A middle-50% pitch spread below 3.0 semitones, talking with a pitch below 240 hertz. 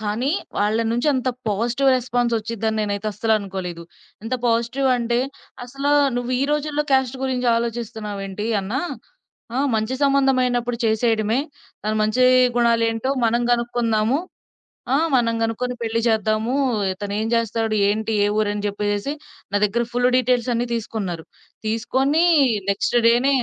Yes: narrow, 2.5 semitones; high, 230 Hz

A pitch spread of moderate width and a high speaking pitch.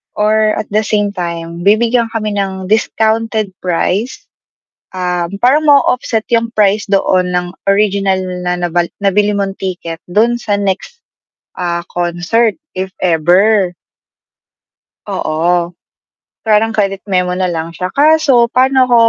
Yes: average, 3.8 semitones; high, 200 Hz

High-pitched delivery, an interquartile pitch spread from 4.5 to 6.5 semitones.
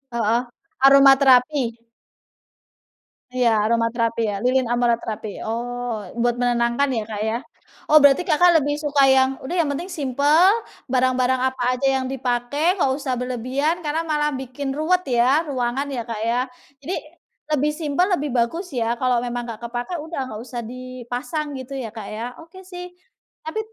No: very high, 260 Hz; average, 3.6 semitones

